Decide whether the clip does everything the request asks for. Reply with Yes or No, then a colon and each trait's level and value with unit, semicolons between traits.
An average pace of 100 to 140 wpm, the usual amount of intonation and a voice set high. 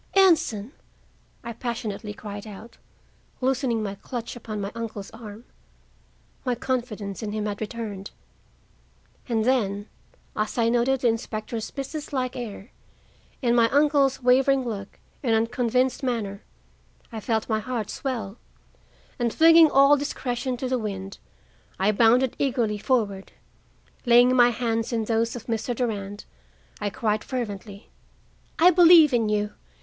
Yes: slow, 135 wpm; average, 3.3 semitones; high, 230 Hz